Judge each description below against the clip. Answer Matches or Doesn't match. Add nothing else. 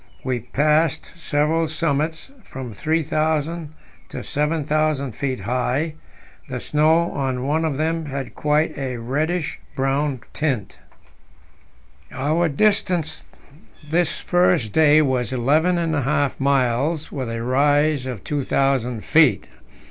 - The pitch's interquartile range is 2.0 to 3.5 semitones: Matches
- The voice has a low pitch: Doesn't match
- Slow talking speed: Matches